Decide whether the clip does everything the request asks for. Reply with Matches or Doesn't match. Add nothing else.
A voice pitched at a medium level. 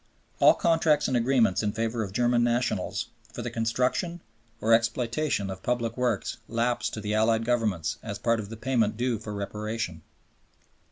Doesn't match